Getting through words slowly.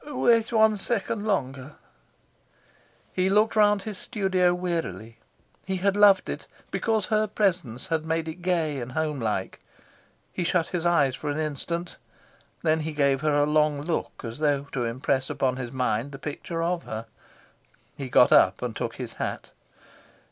No: average, 160 wpm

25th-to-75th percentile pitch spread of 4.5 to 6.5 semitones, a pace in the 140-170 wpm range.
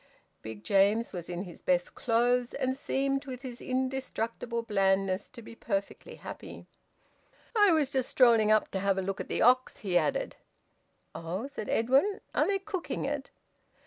Yes: average, 5.1 semitones; average, 165 wpm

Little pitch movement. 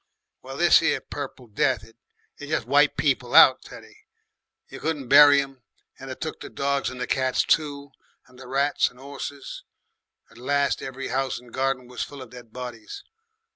Yes: narrow, 2.2 semitones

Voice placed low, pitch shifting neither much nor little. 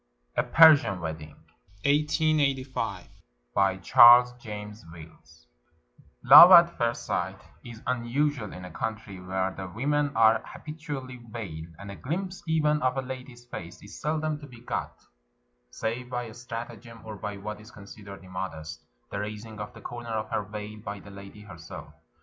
Yes: low, 110 Hz; average, 4.4 semitones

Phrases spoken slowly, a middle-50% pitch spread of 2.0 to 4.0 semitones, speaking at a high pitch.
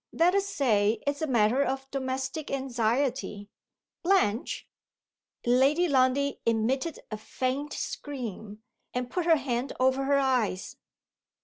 Yes: slow, 125 wpm; average, 3.1 semitones; very high, 265 Hz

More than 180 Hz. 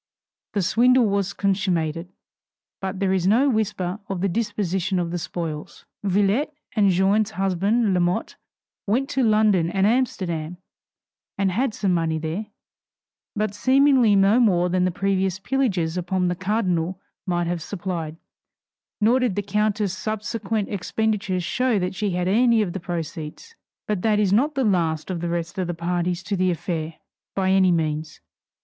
Yes: high, 190 Hz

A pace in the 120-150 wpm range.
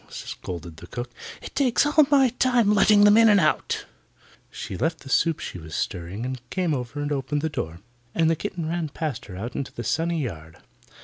No: fast, 205 wpm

